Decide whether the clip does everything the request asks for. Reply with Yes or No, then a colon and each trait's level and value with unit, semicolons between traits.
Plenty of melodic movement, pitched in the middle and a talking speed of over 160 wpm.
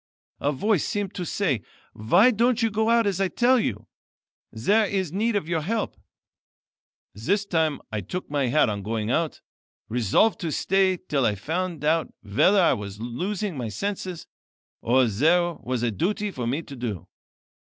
Yes: wide, 8.8 semitones; medium, 165 Hz; average, 175 wpm